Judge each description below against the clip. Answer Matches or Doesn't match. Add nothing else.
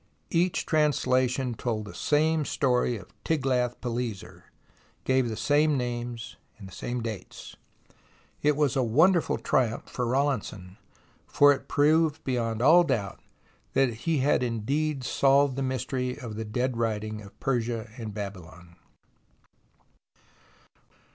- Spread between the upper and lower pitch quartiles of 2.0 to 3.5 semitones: Doesn't match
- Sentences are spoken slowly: Matches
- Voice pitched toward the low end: Matches